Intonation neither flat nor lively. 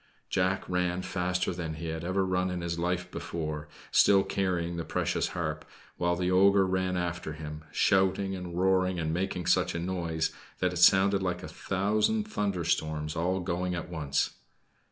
No: narrow, 1.9 semitones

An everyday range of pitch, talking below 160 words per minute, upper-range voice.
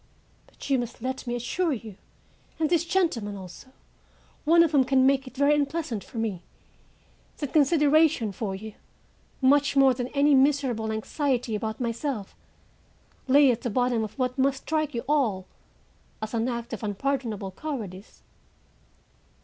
Yes: average, 4.3 semitones; average, 150 wpm; very high, 255 Hz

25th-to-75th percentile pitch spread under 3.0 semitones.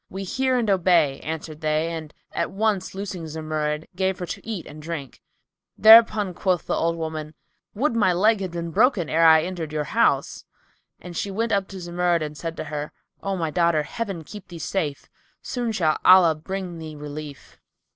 No: average, 3.8 semitones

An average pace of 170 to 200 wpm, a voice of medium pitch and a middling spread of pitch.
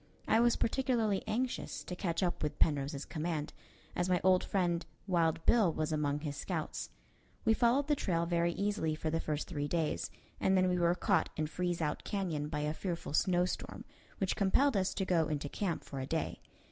Yes: average, 195 wpm; medium, 175 Hz; average, 3.8 semitones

